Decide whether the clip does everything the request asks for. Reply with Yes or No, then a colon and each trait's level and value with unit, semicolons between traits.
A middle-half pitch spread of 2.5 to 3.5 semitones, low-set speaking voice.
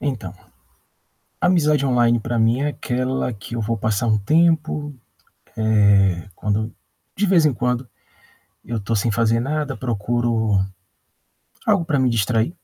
No: average, 4.7 semitones; low, 120 Hz